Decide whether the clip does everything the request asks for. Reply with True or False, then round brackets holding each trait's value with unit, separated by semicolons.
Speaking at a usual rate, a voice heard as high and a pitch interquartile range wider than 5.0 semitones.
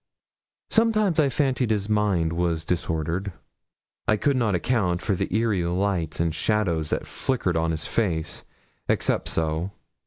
False (145 wpm; 95 Hz; 5.4 semitones)